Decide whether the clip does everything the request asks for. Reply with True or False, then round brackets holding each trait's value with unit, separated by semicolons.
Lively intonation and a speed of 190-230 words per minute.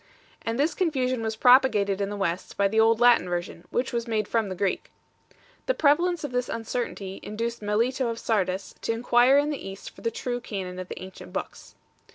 False (4.0 semitones; 205 wpm)